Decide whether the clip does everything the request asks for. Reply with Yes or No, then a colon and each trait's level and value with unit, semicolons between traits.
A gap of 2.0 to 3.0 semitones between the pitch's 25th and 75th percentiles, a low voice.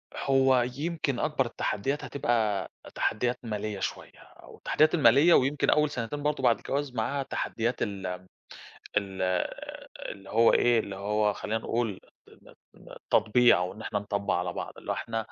No: average, 4.7 semitones; low, 115 Hz